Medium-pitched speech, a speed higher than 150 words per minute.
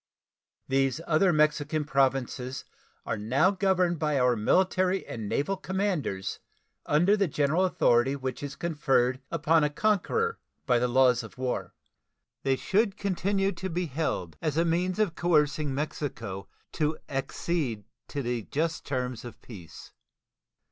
No: medium, 150 Hz; slow, 135 wpm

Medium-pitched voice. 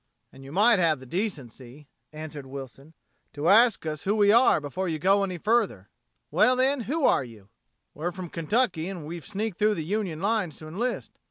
Yes: medium, 175 Hz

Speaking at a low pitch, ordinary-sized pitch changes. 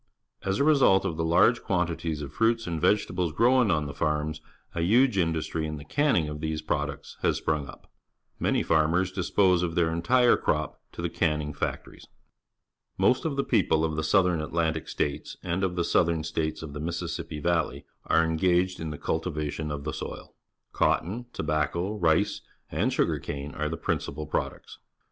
Yes: very low, 80 Hz; average, 3.3 semitones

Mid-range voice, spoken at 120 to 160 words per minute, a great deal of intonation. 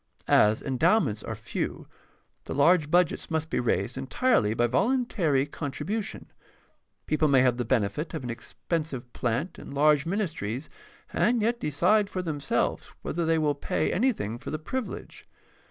Yes: medium, 150 Hz; average, 155 wpm; wide, 6.3 semitones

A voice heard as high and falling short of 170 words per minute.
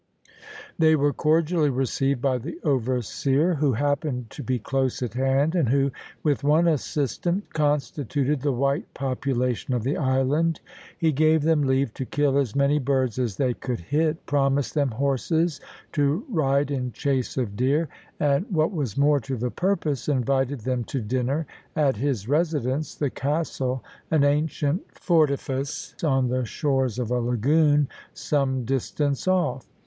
No: medium, 140 Hz; average, 155 wpm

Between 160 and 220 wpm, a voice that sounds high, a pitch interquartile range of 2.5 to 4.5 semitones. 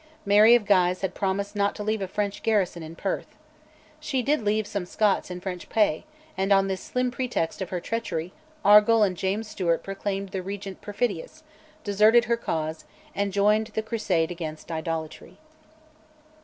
Yes: average, 170 wpm; high, 200 Hz; average, 3.0 semitones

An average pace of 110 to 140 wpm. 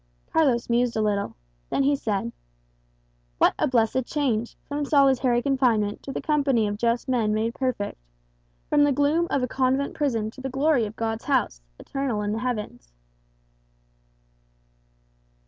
No: average, 150 wpm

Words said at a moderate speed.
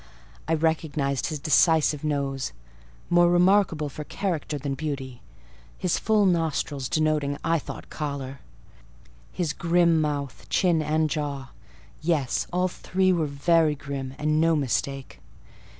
No: slow, 120 wpm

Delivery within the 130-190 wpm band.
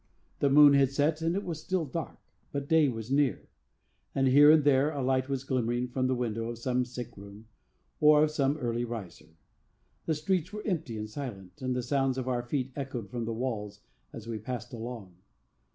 No: average, 200 wpm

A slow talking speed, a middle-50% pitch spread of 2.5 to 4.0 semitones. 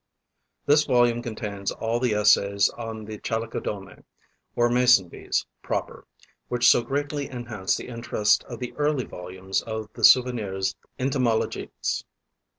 Yes: slow, 130 wpm; average, 3.2 semitones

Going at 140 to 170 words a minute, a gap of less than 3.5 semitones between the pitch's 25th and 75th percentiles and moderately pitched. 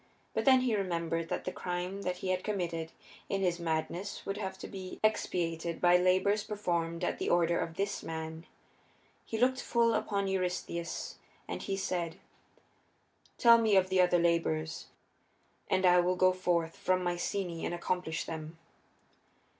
Yes: average, 160 wpm; narrow, 2.6 semitones; medium, 180 Hz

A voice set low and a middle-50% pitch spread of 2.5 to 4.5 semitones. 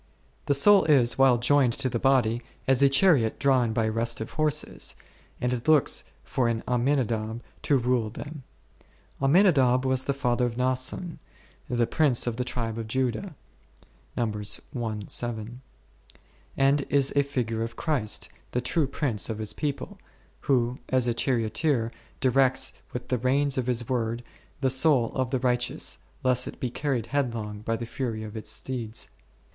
Yes: low, 125 Hz; average, 2.9 semitones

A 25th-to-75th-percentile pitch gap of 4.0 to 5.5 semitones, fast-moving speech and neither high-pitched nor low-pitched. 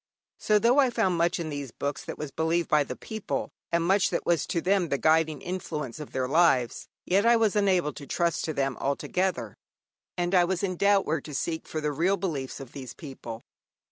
Yes: average, 4.7 semitones; fast, 215 wpm; medium, 165 Hz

